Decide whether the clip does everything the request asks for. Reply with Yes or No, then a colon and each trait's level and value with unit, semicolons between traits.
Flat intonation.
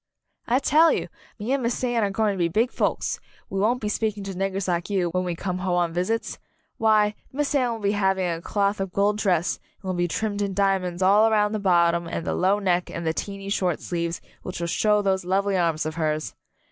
No: average, 3.0 semitones